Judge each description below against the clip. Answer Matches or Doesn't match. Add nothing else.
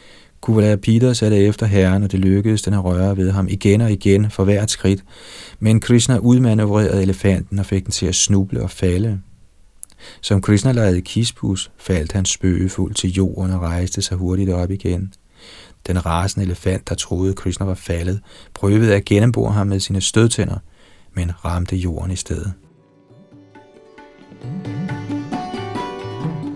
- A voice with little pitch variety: Matches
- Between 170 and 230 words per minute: Doesn't match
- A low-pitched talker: Matches